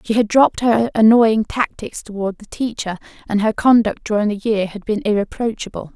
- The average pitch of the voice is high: Yes, high, 215 Hz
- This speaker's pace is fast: No, average, 180 wpm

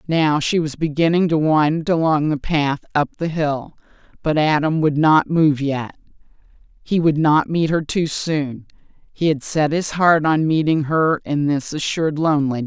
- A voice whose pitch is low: No, medium, 155 Hz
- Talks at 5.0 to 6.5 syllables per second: No, 4.5 syllables/s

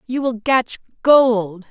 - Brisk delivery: No, average, 140 wpm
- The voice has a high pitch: Yes, high, 235 Hz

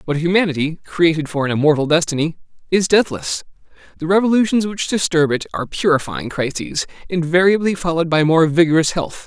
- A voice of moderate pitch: Yes, medium, 165 Hz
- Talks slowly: No, average, 150 wpm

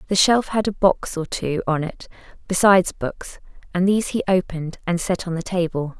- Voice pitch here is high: No, medium, 180 Hz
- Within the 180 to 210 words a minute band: Yes, average, 200 wpm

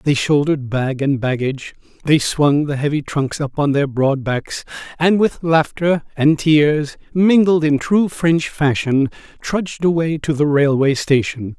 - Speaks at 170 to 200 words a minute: No, average, 160 wpm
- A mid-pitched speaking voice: Yes, medium, 150 Hz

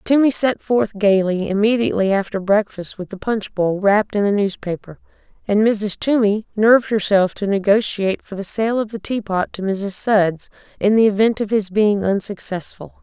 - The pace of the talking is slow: No, average, 175 wpm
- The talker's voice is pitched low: No, high, 205 Hz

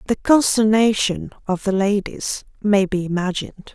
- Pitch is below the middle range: No, high, 205 Hz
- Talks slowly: Yes, slow, 130 wpm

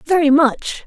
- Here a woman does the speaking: Yes, female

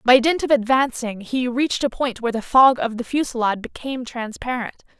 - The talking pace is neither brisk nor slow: Yes, average, 190 wpm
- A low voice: No, high, 245 Hz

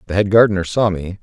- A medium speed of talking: No, fast, 245 wpm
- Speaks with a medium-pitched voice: No, very low, 95 Hz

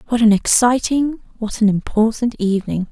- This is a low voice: No, high, 225 Hz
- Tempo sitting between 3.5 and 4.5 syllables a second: No, 5.1 syllables/s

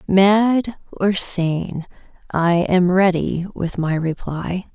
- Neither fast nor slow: No, slow, 115 wpm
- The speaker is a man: No, female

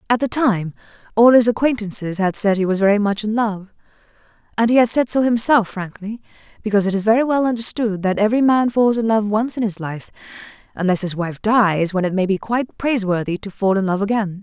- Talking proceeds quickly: Yes, fast, 210 wpm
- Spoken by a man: No, female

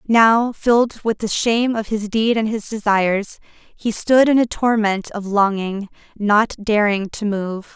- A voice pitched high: Yes, high, 215 Hz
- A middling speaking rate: Yes, average, 170 wpm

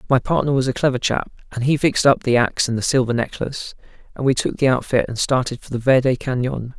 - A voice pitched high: No, low, 130 Hz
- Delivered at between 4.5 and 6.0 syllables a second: No, 6.4 syllables/s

